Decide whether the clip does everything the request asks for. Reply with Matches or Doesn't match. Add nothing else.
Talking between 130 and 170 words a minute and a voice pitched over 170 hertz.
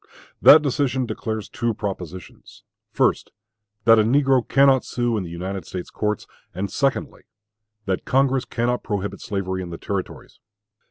Doesn't match